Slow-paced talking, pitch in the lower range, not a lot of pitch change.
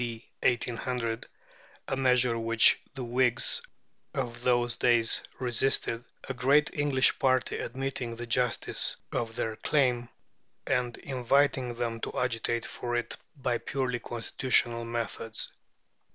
Yes: slow, 120 wpm; low, 120 Hz; narrow, 1.8 semitones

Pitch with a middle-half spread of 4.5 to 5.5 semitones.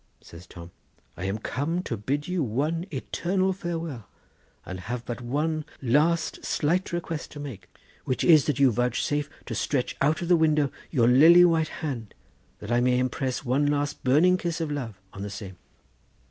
Yes: average, 5.2 semitones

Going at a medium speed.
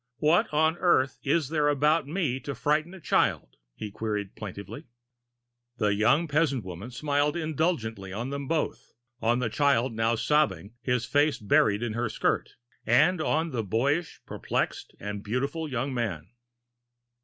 Yes: average, 150 wpm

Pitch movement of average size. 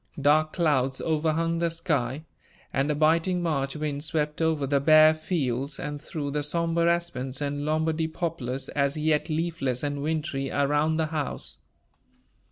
No: narrow, 2.3 semitones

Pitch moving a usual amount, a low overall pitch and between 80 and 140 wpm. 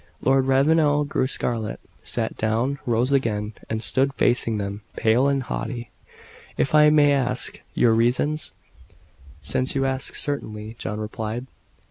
Yes: average, 3.8 semitones; low, 130 Hz; slow, 135 wpm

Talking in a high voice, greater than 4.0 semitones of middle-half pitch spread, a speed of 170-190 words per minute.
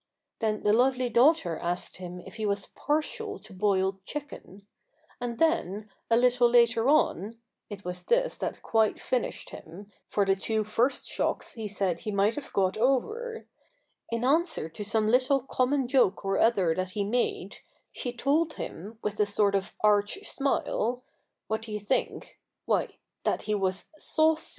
Yes: high, 220 Hz; average, 4.5 semitones; average, 175 wpm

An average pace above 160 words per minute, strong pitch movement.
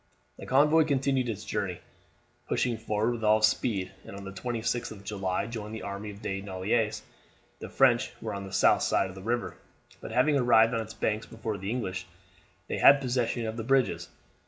No: average, 195 wpm; average, 3.4 semitones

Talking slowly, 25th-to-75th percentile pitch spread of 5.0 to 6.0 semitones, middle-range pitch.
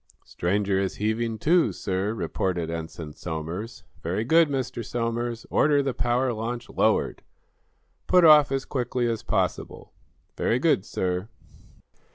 No: slow, 130 wpm; average, 5.3 semitones; low, 115 Hz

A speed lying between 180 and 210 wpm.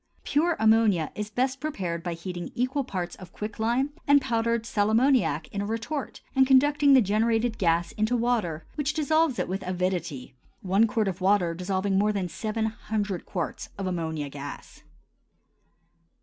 No: average, 160 wpm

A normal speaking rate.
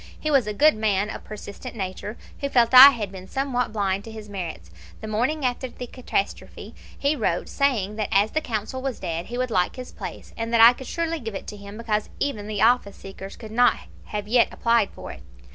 No: fast, 225 wpm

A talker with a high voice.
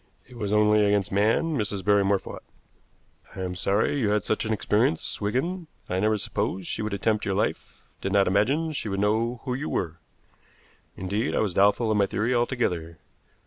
No: low, 105 Hz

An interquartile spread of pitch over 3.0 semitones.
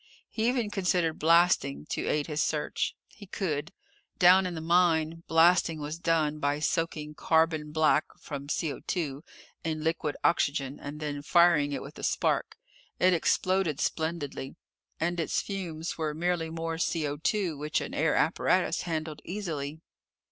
No: narrow, 2.4 semitones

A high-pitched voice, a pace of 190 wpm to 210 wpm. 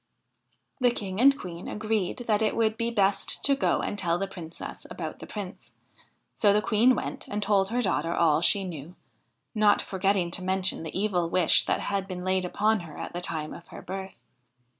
Yes: high, 195 Hz; average, 200 wpm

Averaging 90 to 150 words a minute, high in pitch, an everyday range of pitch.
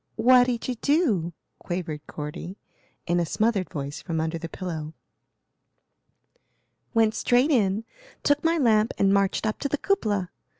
No: average, 145 wpm; high, 200 Hz; wide, 6.4 semitones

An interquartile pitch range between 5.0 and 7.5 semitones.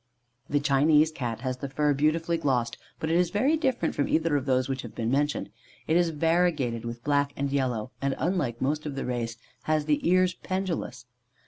No: average, 4.1 semitones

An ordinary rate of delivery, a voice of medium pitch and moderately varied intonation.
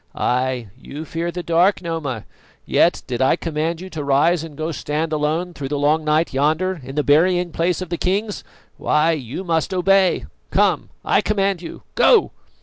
Yes: average, 175 wpm; medium, 160 Hz; average, 3.2 semitones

